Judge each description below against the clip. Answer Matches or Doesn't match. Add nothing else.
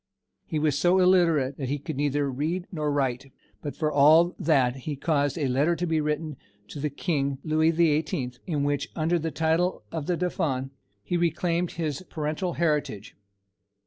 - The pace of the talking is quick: Doesn't match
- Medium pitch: Matches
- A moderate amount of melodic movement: Matches